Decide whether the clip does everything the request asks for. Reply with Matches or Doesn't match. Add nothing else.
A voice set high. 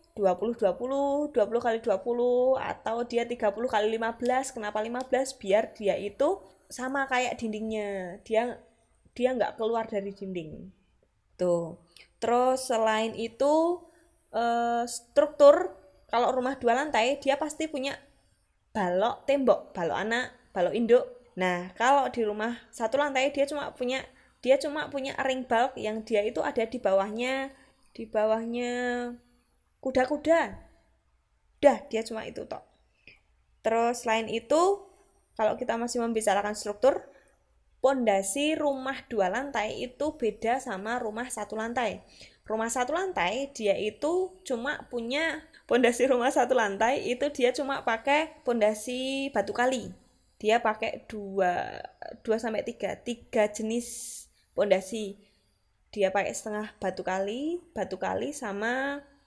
Matches